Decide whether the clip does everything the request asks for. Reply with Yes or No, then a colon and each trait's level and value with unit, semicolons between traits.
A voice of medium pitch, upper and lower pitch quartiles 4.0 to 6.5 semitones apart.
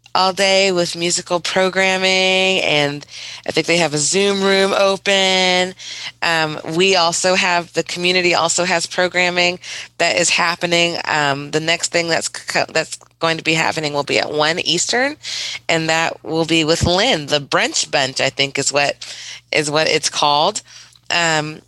No: medium, 170 Hz; average, 2.9 semitones